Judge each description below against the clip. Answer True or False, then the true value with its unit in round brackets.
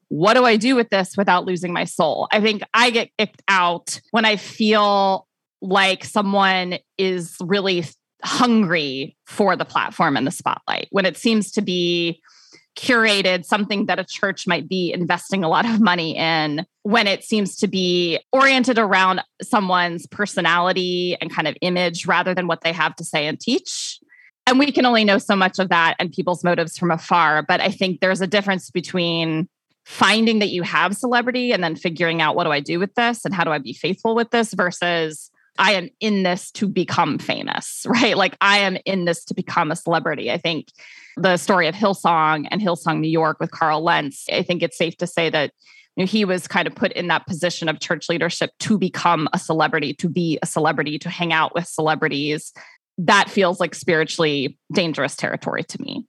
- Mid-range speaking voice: True (180 Hz)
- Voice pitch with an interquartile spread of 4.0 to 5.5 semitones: False (3.3 semitones)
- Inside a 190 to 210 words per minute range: True (200 wpm)